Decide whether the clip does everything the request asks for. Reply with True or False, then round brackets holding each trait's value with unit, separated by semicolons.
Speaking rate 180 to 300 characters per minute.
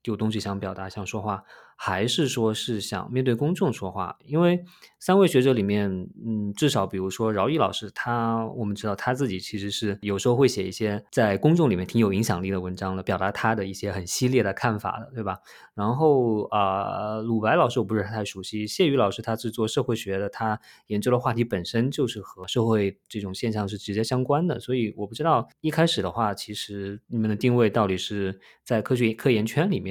False (325 characters per minute)